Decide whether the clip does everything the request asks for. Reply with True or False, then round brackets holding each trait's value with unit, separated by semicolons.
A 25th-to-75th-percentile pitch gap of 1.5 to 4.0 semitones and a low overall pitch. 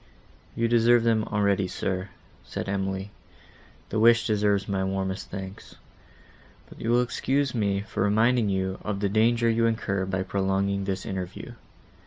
True (3.0 semitones; 100 Hz)